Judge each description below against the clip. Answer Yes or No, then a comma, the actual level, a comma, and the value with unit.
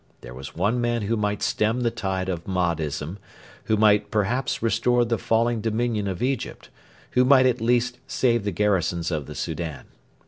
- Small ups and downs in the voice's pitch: No, average, 4.9 semitones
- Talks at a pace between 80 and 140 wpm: No, average, 175 wpm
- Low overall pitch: Yes, low, 105 Hz